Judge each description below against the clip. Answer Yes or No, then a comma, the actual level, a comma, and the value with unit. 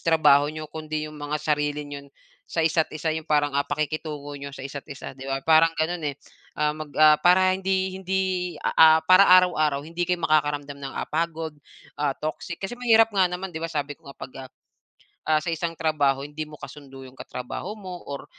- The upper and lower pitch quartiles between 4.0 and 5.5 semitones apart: No, narrow, 2.6 semitones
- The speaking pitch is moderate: Yes, medium, 155 Hz